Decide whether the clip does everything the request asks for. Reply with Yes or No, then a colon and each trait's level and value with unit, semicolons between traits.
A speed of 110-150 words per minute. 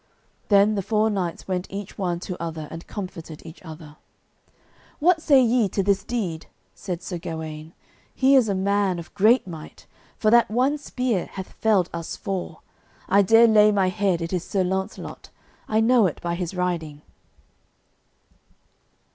No: average, 165 wpm